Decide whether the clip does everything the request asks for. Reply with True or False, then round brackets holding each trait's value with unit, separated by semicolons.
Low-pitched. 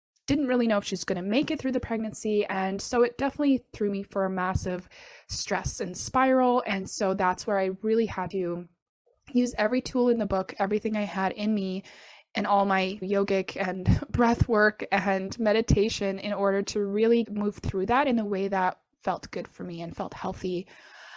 False (205 Hz)